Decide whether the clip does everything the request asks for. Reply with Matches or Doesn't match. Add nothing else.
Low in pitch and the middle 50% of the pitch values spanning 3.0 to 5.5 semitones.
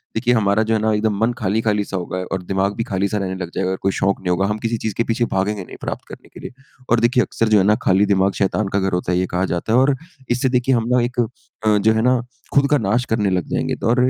Matches